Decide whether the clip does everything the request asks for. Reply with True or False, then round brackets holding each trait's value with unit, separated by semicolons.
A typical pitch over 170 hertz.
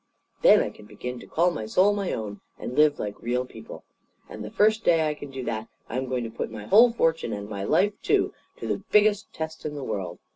False (135 Hz)